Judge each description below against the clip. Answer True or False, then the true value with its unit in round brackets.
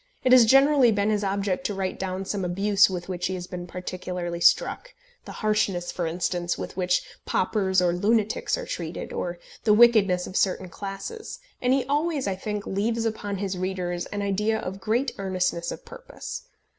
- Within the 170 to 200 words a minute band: True (180 wpm)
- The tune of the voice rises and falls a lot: False (3.2 semitones)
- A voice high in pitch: True (195 Hz)